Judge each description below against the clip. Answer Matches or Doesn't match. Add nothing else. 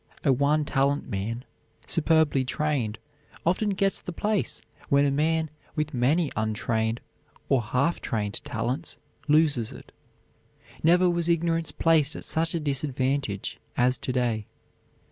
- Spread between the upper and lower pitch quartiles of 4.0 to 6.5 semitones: Matches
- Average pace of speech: Doesn't match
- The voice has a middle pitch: Matches